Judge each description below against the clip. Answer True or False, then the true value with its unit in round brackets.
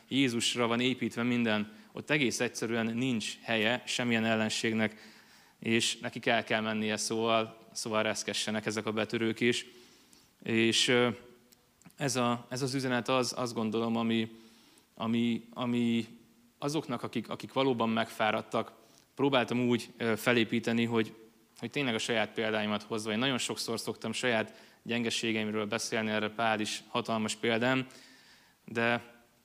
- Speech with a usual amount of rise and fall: False (1.6 semitones)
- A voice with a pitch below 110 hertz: False (115 Hz)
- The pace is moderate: True (130 wpm)